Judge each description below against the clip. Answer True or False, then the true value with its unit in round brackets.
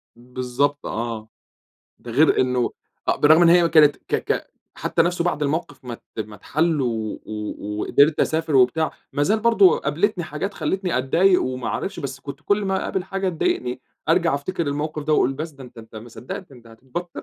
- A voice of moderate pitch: True (145 Hz)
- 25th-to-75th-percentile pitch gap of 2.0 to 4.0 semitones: False (5.3 semitones)